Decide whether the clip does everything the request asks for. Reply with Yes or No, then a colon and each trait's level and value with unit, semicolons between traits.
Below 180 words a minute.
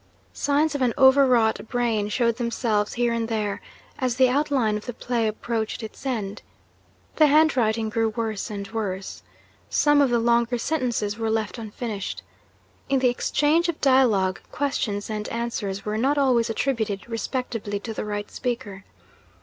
Yes: average, 155 wpm